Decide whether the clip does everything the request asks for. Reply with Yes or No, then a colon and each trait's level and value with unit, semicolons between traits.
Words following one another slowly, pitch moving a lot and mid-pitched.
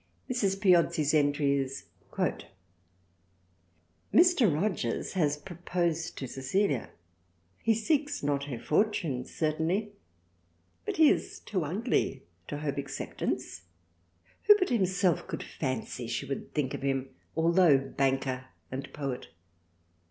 Yes: slow, 120 wpm; wide, 6.1 semitones; medium, 145 Hz